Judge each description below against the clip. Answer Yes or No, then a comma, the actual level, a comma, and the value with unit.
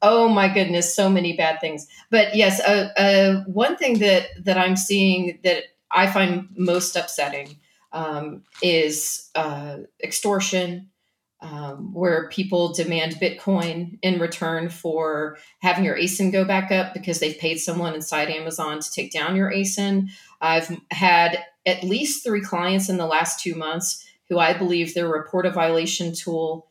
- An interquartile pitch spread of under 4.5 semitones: Yes, average, 3.0 semitones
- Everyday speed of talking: Yes, average, 155 wpm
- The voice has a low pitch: No, medium, 175 Hz